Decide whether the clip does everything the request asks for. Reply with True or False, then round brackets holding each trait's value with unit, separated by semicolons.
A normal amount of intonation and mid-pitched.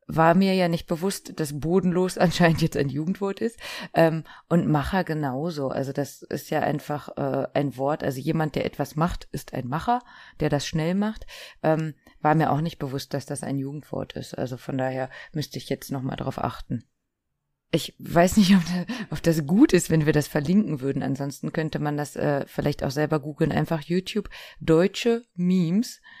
True (3.9 semitones; 160 Hz)